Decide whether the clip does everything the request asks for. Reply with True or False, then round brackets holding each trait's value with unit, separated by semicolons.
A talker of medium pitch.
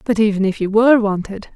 False (210 Hz)